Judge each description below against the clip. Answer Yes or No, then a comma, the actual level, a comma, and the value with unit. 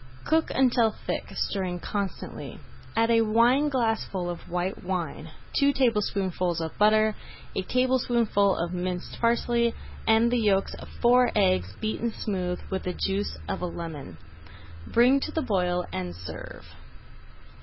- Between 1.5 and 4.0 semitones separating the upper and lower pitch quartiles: No, average, 4.7 semitones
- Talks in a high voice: Yes, high, 205 Hz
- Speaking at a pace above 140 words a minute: No, slow, 135 wpm